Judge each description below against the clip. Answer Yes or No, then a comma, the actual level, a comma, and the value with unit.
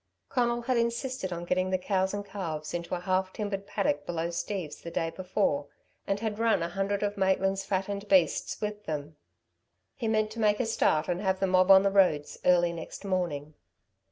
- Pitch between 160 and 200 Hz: Yes, high, 190 Hz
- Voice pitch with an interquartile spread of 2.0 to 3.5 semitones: Yes, average, 3.1 semitones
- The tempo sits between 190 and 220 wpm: Yes, average, 195 wpm